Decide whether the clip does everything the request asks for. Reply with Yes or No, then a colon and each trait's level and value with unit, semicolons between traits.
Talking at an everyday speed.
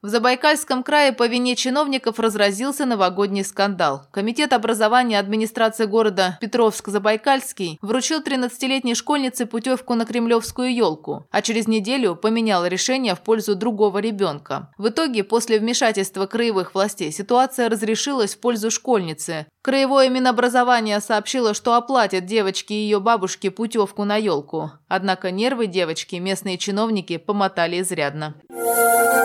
Yes: average, 120 wpm